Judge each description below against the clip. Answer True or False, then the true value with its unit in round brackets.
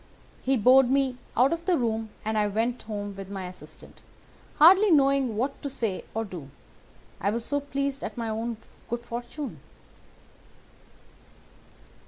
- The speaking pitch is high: True (240 Hz)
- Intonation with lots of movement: False (4.2 semitones)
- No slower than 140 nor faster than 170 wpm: True (150 wpm)